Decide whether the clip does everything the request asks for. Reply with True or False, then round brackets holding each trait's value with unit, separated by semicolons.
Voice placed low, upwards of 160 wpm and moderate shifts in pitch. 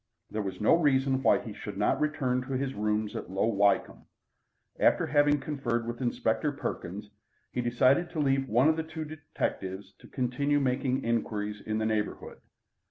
True (125 Hz; 170 wpm; 5.0 semitones)